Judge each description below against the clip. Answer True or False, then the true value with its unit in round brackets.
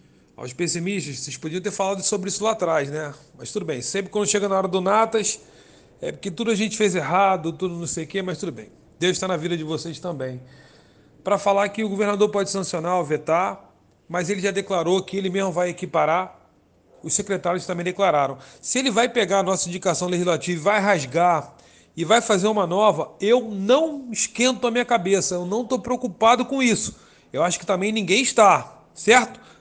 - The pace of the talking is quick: True (200 wpm)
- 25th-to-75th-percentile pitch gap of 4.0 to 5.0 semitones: False (3.3 semitones)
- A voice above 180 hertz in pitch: True (190 Hz)